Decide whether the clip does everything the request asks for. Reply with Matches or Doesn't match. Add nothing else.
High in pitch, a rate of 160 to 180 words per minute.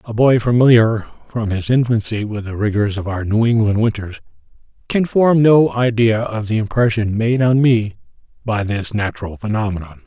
Doesn't match